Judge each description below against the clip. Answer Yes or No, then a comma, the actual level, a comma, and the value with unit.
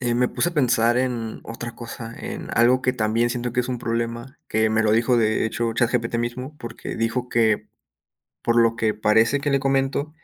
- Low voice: Yes, low, 120 Hz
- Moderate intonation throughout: No, narrow, 1.7 semitones